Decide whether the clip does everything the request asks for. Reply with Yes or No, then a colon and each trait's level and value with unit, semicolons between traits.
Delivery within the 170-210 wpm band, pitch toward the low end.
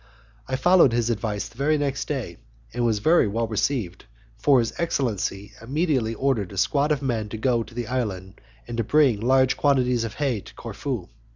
Yes: average, 185 wpm; low, 120 Hz